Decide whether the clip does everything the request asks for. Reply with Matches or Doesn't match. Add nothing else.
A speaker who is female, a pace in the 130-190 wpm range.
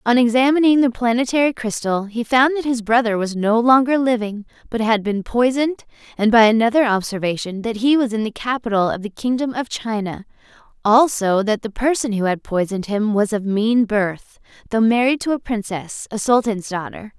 Matches